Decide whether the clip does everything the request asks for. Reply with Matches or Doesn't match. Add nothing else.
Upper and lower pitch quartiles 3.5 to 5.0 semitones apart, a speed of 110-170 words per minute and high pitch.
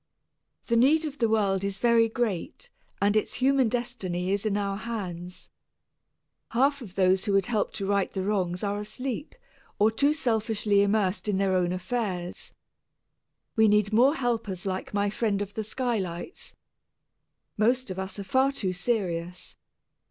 Matches